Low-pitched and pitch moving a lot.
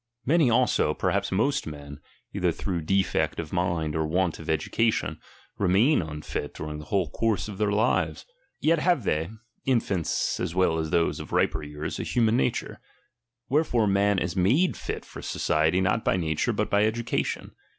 Yes: very low, 95 Hz; wide, 6.1 semitones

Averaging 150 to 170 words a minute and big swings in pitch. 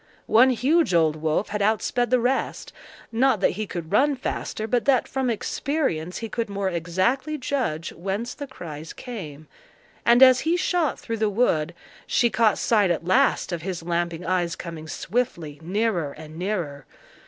Yes: average, 165 wpm; wide, 6.6 semitones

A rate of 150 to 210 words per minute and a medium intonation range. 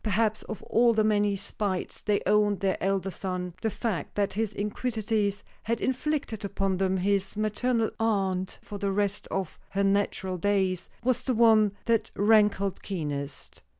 No: average, 155 wpm; narrow, 2.2 semitones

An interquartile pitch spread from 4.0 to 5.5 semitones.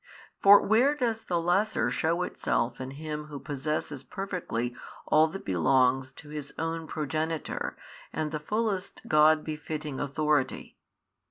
No: average, 3.6 semitones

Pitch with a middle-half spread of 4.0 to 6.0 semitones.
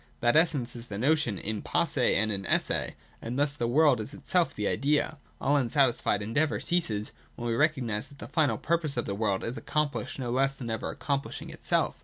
Yes: average, 4.6 semitones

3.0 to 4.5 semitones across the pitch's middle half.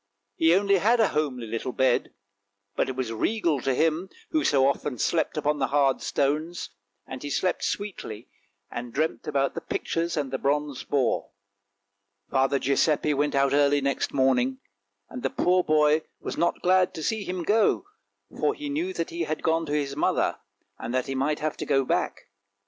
Yes: average, 4.2 semitones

